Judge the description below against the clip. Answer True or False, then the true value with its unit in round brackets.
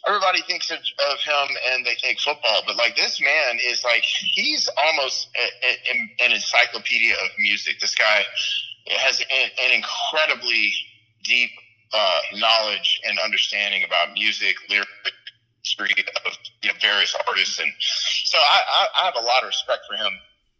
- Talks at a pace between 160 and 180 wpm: True (165 wpm)